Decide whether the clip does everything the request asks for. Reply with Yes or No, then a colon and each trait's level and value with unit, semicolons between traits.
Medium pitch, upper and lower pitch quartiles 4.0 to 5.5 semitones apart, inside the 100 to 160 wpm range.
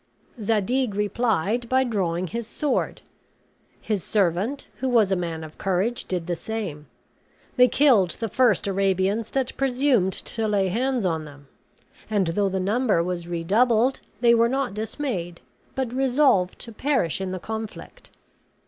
No: high, 210 Hz; average, 5.1 semitones; average, 150 wpm